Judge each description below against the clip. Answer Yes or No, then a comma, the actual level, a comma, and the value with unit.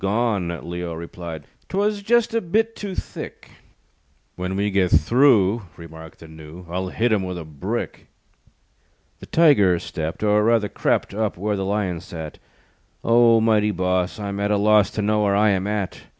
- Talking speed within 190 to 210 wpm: No, average, 170 wpm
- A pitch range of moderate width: Yes, average, 3.8 semitones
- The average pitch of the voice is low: Yes, low, 100 Hz